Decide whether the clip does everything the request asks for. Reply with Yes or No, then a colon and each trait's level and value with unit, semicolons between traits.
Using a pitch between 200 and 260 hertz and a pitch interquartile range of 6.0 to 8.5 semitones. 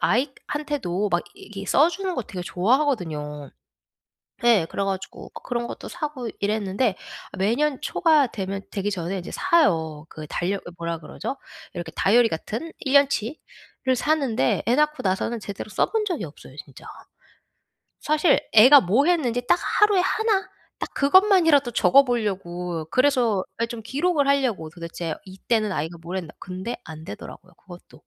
Yes: high, 225 Hz; wide, 7.8 semitones